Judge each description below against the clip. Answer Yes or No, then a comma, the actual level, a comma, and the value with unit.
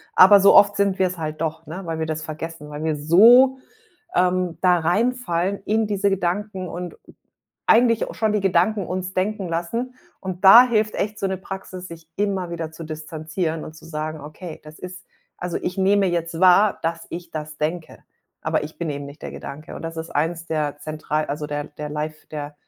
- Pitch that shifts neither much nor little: Yes, average, 3.7 semitones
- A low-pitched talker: No, medium, 170 Hz